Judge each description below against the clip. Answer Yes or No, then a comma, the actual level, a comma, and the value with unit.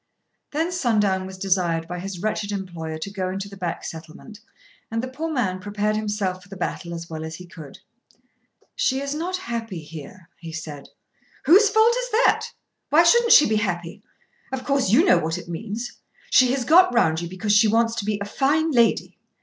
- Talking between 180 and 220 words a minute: Yes, average, 200 wpm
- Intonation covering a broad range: Yes, wide, 6.9 semitones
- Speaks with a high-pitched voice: Yes, high, 205 Hz